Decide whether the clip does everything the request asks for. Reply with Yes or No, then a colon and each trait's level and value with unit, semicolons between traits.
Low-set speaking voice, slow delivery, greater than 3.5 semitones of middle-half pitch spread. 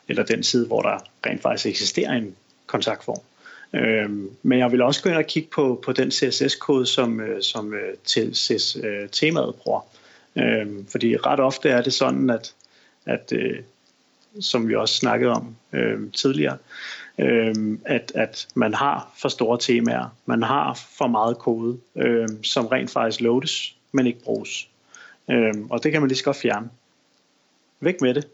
No: low, 120 Hz; slow, 140 wpm; average, 3.2 semitones